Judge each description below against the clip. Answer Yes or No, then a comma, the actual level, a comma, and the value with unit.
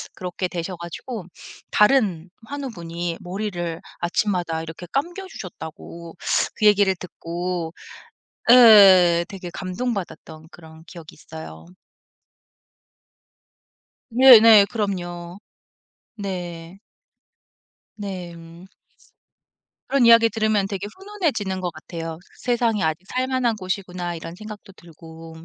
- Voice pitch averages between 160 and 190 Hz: Yes, medium, 185 Hz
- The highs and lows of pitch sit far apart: No, average, 4.1 semitones